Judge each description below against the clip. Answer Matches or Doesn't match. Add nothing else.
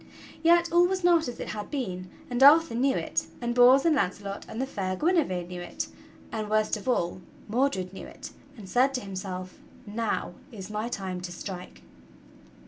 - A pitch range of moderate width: Doesn't match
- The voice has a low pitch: Doesn't match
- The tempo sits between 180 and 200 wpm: Matches